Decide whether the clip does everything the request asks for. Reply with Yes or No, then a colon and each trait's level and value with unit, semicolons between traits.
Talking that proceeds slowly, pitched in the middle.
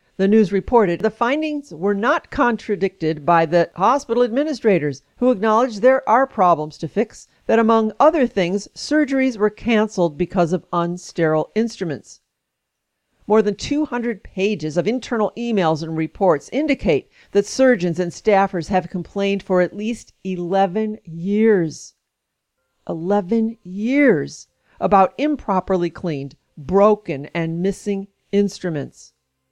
No: slow, 120 wpm; high, 200 Hz